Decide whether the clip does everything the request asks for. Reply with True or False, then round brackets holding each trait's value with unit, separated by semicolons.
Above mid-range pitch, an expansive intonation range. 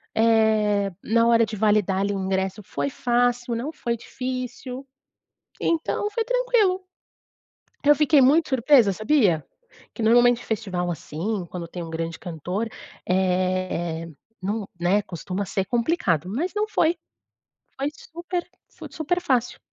True (225 Hz; 6.3 semitones)